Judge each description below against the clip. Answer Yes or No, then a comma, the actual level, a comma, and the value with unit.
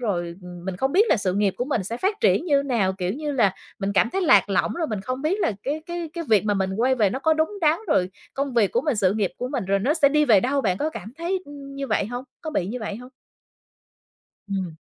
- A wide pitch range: Yes, wide, 7.2 semitones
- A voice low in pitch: No, high, 245 Hz